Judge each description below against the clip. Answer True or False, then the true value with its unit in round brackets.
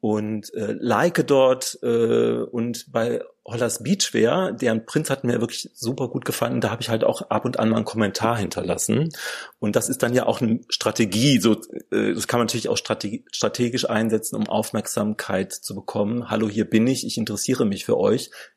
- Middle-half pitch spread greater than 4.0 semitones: False (2.8 semitones)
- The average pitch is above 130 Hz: False (115 Hz)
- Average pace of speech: False (195 wpm)